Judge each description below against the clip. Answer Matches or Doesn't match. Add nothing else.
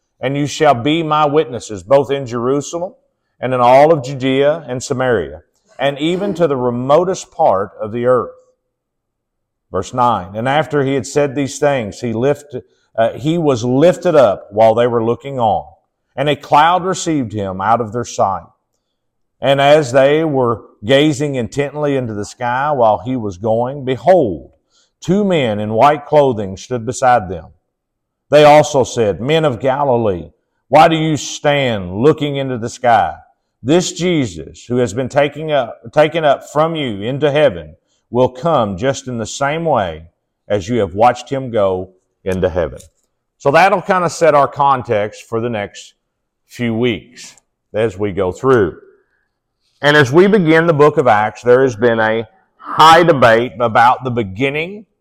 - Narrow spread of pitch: Doesn't match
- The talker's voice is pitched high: Doesn't match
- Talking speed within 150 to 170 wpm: Matches